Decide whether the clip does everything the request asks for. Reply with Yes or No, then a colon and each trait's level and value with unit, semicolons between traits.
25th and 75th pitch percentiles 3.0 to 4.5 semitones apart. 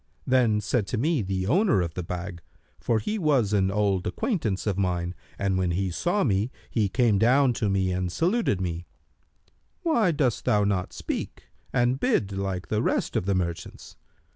No: wide, 5.4 semitones